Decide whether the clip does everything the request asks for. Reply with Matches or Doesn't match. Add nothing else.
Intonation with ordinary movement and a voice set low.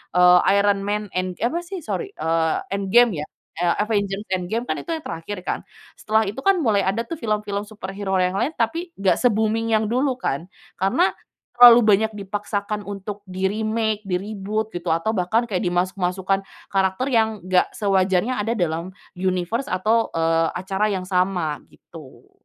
Doesn't match